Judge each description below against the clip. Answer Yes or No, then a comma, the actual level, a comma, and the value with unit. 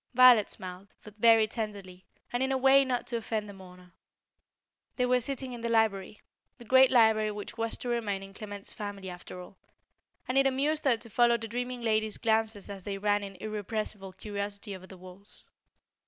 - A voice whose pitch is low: No, high, 215 Hz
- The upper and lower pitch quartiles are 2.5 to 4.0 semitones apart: Yes, average, 3.3 semitones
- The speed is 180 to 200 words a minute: Yes, average, 190 wpm